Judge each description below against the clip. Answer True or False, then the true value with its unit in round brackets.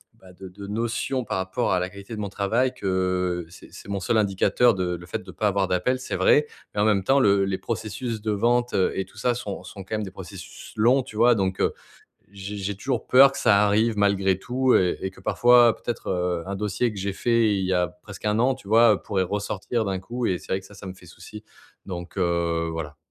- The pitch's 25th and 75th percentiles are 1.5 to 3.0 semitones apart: False (3.6 semitones)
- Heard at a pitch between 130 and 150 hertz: False (100 Hz)